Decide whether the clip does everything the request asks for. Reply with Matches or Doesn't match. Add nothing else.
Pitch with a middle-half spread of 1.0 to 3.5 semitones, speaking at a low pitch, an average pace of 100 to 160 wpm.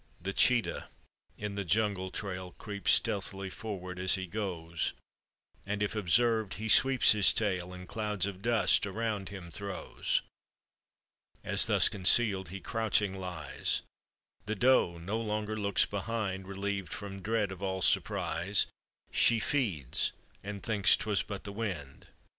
Matches